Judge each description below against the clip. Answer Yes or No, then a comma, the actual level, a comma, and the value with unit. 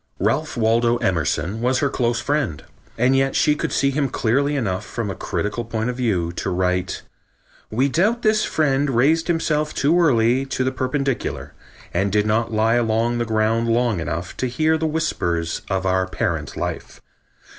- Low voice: Yes, low, 120 Hz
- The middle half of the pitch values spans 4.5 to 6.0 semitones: Yes, average, 5.0 semitones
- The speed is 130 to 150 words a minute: No, average, 175 wpm